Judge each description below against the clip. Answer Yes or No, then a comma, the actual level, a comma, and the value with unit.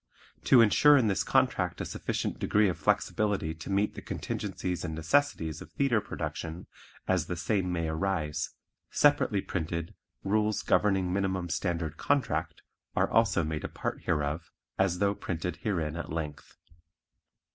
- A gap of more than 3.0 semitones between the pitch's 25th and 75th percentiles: Yes, average, 4.2 semitones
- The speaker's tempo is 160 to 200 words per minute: No, average, 145 wpm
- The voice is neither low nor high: No, very low, 90 Hz